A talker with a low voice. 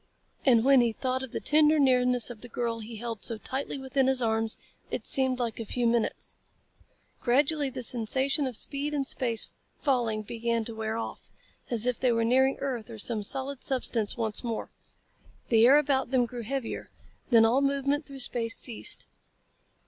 No: high, 245 Hz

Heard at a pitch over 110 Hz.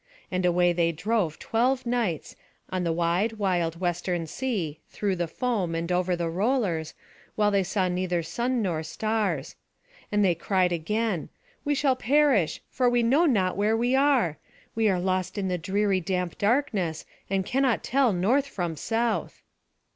Yes: high, 190 Hz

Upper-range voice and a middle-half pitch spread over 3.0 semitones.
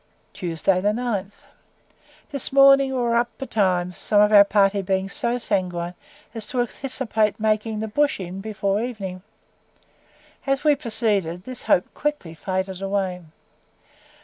Yes: high, 210 Hz; average, 4.2 semitones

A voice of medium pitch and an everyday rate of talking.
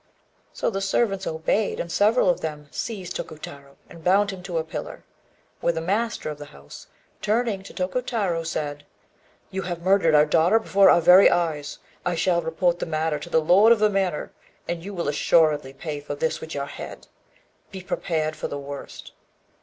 Yes: medium, 170 Hz; average, 185 wpm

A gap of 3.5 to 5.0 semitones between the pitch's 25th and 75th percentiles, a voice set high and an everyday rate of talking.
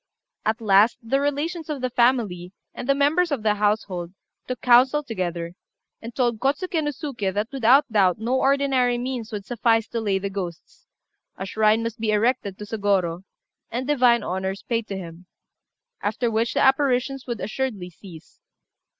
Yes: average, 4.7 semitones; high, 230 Hz; average, 165 wpm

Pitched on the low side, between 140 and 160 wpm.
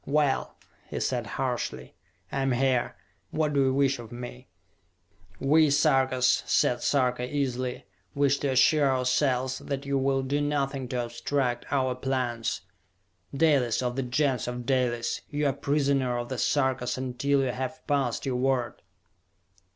Yes: low, 130 Hz; average, 150 wpm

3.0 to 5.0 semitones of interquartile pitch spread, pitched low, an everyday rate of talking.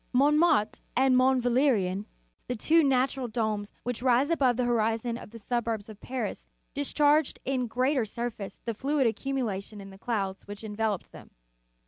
No: average, 3.7 semitones; high, 240 Hz; average, 165 wpm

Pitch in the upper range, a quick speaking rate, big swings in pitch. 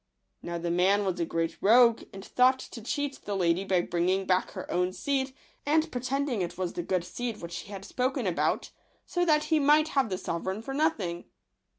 Yes: high, 205 Hz; fast, 210 wpm; wide, 7.0 semitones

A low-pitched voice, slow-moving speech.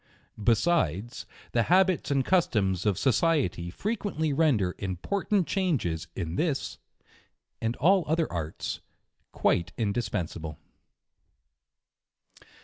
Yes: low, 120 Hz; slow, 95 wpm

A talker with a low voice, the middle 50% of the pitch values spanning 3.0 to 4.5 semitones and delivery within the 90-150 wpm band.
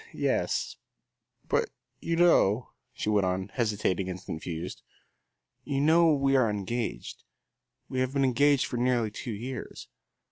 No: low, 120 Hz; average, 5.2 semitones; slow, 135 wpm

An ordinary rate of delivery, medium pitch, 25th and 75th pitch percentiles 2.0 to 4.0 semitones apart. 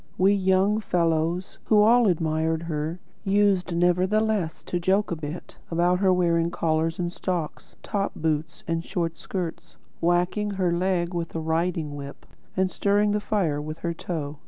Yes: average, 160 wpm; medium, 175 Hz; average, 2.7 semitones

